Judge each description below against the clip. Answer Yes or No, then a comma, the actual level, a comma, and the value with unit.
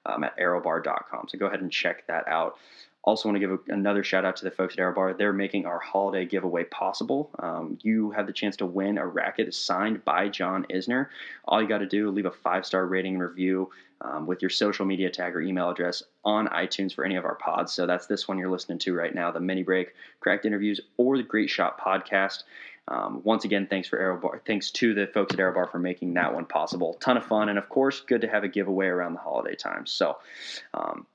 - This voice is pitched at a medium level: No, very low, 95 Hz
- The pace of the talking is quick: Yes, fast, 245 wpm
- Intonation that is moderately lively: No, narrow, 1.8 semitones